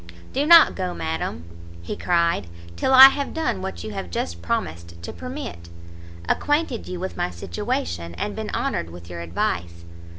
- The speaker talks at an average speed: Yes, average, 165 wpm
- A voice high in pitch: No, very low, 90 Hz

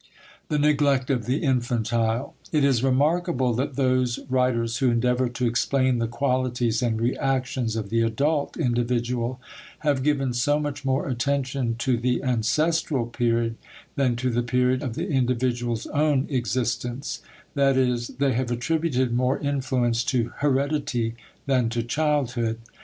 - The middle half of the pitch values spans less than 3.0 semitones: Yes, narrow, 2.6 semitones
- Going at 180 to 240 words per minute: No, average, 140 wpm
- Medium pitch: No, low, 125 Hz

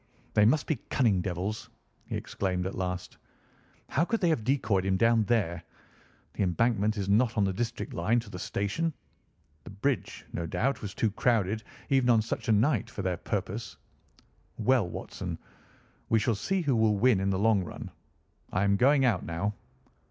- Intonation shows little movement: No, average, 4.1 semitones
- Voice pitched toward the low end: Yes, low, 110 Hz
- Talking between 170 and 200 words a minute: Yes, average, 180 wpm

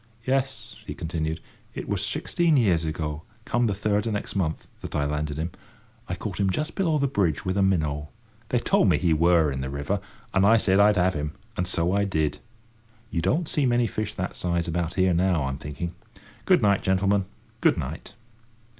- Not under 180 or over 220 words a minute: Yes, average, 200 wpm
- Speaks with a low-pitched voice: Yes, very low, 95 Hz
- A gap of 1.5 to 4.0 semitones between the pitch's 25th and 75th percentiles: No, average, 4.7 semitones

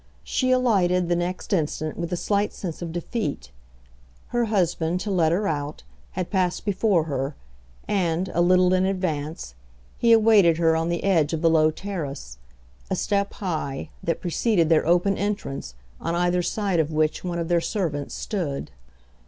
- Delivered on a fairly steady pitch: No, average, 3.6 semitones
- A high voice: No, medium, 175 Hz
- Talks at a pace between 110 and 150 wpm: No, average, 170 wpm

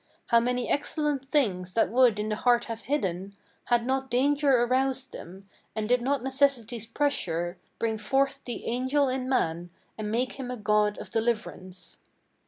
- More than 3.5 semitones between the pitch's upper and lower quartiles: Yes, average, 4.0 semitones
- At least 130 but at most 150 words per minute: No, average, 165 wpm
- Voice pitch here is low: No, high, 240 Hz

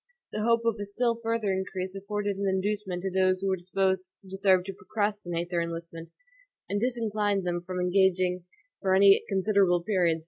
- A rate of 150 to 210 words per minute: Yes, average, 175 wpm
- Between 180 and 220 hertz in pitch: Yes, high, 190 Hz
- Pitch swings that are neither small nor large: No, narrow, 2.1 semitones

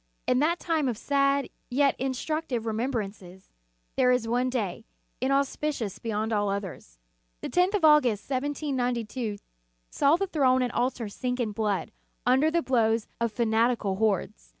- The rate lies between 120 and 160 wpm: Yes, average, 150 wpm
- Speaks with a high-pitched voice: Yes, very high, 250 Hz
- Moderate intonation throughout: Yes, average, 4.1 semitones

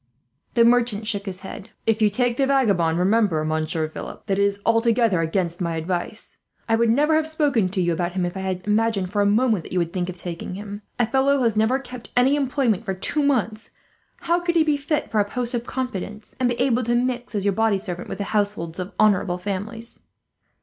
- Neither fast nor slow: No, fast, 230 wpm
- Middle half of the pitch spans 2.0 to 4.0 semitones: No, average, 4.7 semitones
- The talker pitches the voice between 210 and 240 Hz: Yes, high, 215 Hz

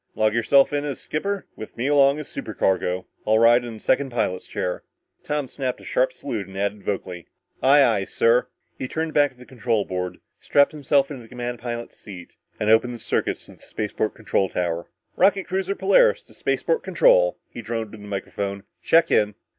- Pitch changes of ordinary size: No, wide, 5.7 semitones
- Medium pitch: No, low, 120 Hz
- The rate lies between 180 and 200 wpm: Yes, average, 195 wpm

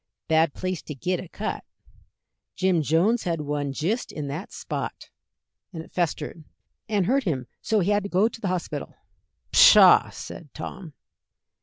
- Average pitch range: Yes, average, 4.5 semitones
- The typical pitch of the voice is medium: Yes, medium, 175 Hz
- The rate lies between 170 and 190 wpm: No, average, 160 wpm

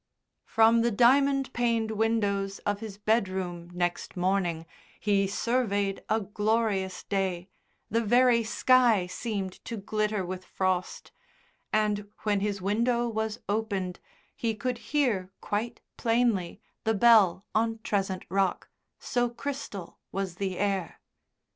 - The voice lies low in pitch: No, high, 210 Hz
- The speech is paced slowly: Yes, slow, 120 wpm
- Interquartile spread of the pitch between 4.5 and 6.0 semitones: No, average, 3.2 semitones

